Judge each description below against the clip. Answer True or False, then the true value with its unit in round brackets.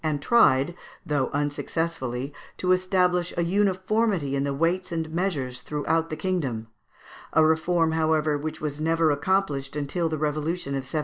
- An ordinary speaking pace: True (150 wpm)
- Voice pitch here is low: False (160 Hz)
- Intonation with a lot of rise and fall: False (3.7 semitones)